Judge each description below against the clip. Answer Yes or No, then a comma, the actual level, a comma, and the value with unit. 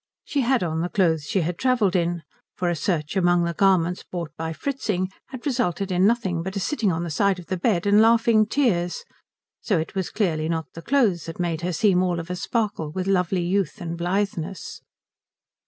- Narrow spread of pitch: No, average, 3.2 semitones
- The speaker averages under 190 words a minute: No, fast, 205 wpm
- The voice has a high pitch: No, medium, 180 Hz